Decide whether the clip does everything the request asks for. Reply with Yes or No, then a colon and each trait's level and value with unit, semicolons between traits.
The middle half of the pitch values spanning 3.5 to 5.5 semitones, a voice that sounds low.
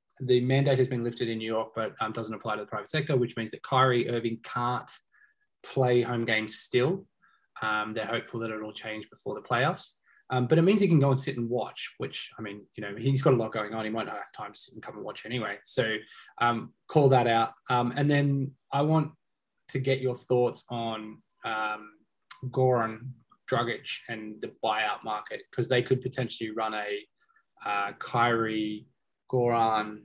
No: average, 3.0 semitones; low, 120 Hz